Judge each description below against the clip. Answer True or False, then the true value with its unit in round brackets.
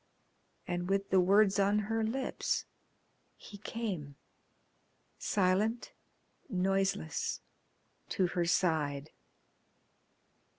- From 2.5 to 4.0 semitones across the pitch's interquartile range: True (3.0 semitones)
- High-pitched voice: True (195 Hz)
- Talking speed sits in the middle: False (80 wpm)